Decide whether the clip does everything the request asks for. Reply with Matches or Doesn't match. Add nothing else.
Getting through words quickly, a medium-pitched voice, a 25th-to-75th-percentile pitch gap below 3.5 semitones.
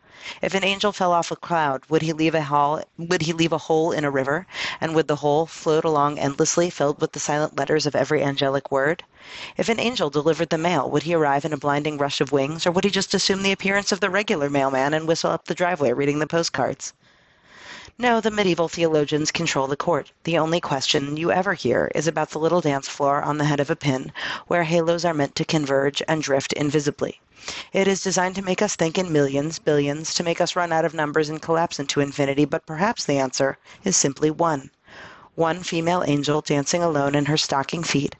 Matches